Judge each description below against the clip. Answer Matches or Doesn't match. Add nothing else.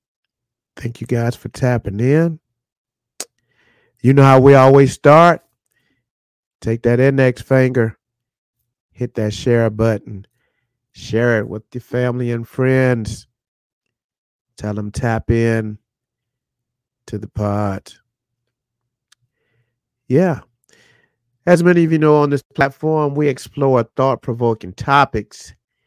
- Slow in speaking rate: Matches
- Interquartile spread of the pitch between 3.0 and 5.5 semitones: Doesn't match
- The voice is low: Matches